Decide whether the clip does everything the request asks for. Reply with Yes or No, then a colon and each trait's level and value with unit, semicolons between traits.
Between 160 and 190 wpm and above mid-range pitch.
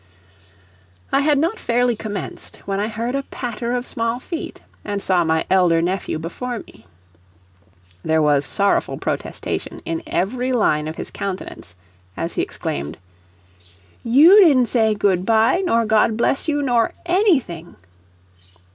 No: average, 140 wpm; high, 225 Hz